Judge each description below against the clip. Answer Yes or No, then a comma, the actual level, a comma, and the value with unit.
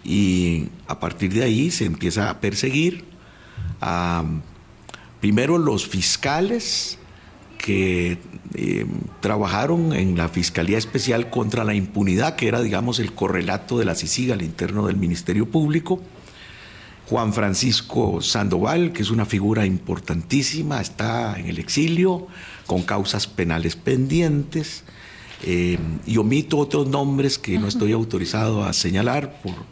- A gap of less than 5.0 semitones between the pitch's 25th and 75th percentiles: No, wide, 5.4 semitones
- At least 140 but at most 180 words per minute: No, average, 130 wpm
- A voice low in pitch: Yes, low, 105 Hz